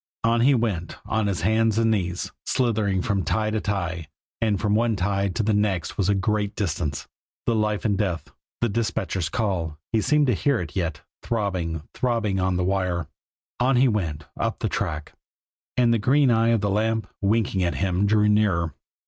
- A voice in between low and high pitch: No, low, 105 Hz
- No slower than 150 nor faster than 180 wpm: No, average, 190 wpm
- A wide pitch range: No, average, 3.7 semitones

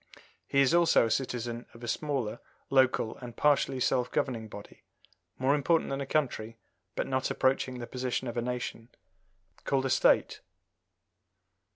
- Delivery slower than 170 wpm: Yes, average, 155 wpm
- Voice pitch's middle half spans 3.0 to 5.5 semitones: No, narrow, 2.5 semitones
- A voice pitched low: Yes, low, 130 Hz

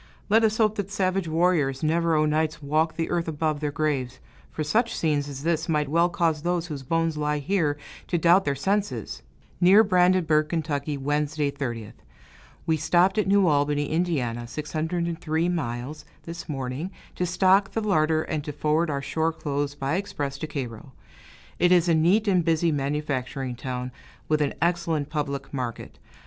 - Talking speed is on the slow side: No, average, 170 wpm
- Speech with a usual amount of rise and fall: Yes, average, 3.2 semitones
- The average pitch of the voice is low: No, medium, 155 Hz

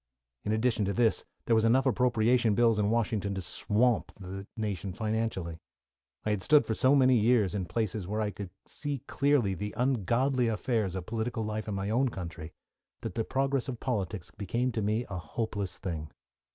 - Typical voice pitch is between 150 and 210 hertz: No, low, 110 Hz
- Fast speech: No, average, 185 wpm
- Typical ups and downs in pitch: Yes, average, 3.5 semitones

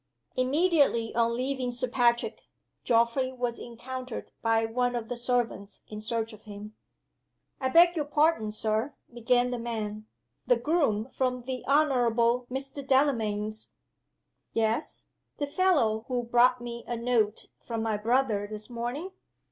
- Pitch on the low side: No, high, 240 Hz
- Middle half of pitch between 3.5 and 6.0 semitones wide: No, average, 2.7 semitones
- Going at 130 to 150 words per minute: Yes, average, 140 wpm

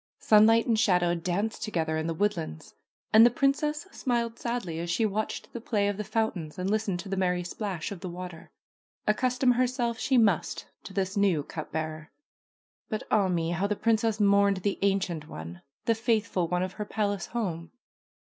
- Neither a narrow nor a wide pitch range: Yes, average, 4.3 semitones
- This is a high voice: Yes, high, 200 Hz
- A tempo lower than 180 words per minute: No, average, 185 wpm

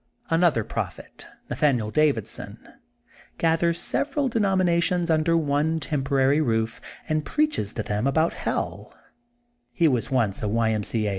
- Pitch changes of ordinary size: No, wide, 6.6 semitones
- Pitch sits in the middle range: Yes, medium, 150 Hz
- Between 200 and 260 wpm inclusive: No, slow, 135 wpm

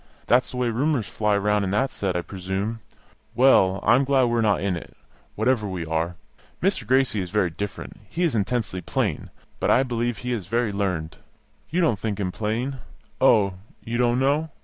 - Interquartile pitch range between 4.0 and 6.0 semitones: Yes, average, 4.4 semitones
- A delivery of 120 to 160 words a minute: No, average, 195 wpm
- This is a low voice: Yes, low, 110 Hz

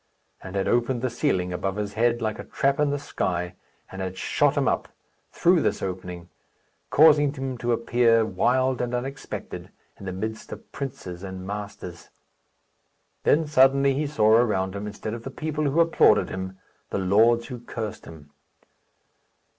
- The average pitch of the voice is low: Yes, low, 115 Hz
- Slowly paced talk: No, average, 165 wpm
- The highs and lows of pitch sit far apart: Yes, wide, 5.7 semitones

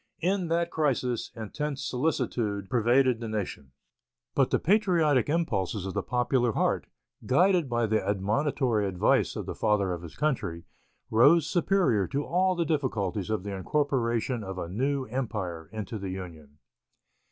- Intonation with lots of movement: Yes, wide, 6.7 semitones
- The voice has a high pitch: No, low, 120 Hz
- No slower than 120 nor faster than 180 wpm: Yes, average, 150 wpm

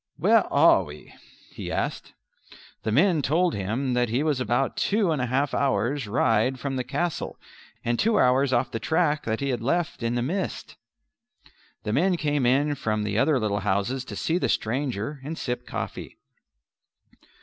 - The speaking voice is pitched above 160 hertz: No, low, 130 Hz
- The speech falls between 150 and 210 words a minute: Yes, average, 175 wpm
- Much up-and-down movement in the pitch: No, average, 4.3 semitones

